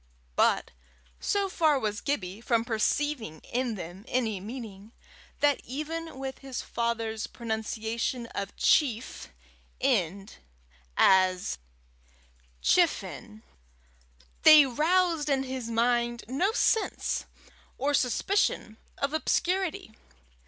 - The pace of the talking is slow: Yes, slow, 95 wpm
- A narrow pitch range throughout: No, average, 5.0 semitones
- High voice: Yes, high, 245 Hz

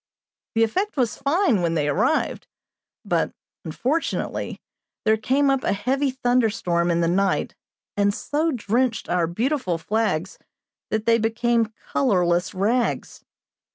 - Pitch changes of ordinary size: No, wide, 5.8 semitones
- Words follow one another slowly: Yes, slow, 125 wpm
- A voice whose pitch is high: Yes, high, 225 Hz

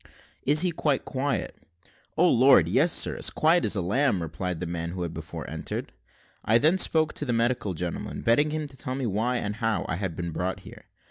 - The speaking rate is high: Yes, fast, 210 wpm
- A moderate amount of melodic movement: No, wide, 8.2 semitones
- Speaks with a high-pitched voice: No, low, 115 Hz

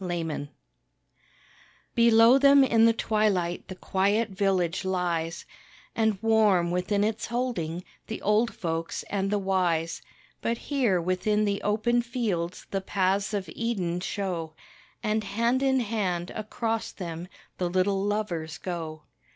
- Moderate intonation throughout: Yes, average, 4.1 semitones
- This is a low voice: No, high, 200 Hz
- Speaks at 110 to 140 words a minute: Yes, slow, 135 wpm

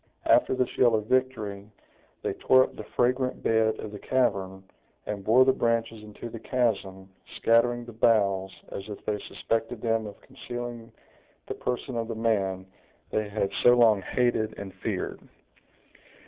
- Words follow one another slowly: No, average, 160 wpm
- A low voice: Yes, low, 115 Hz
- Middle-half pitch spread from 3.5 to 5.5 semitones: No, average, 2.9 semitones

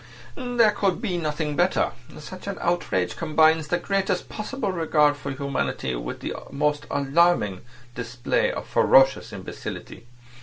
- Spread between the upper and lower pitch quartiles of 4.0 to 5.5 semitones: Yes, average, 4.9 semitones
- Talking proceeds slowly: Yes, slow, 130 wpm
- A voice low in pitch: No, medium, 155 Hz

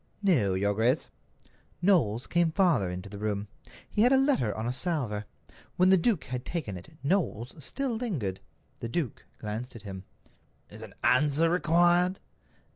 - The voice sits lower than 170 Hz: Yes, medium, 140 Hz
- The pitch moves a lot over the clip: Yes, wide, 9.0 semitones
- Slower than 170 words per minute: Yes, average, 160 wpm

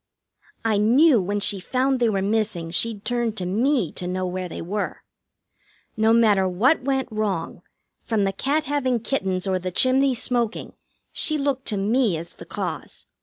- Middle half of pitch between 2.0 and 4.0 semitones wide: No, average, 5.2 semitones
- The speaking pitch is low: No, high, 220 Hz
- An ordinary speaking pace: Yes, average, 170 wpm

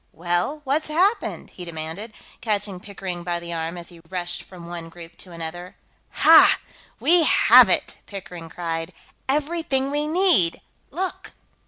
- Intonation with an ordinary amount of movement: No, wide, 8.5 semitones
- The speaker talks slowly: No, average, 145 wpm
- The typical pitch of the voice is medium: Yes, medium, 180 Hz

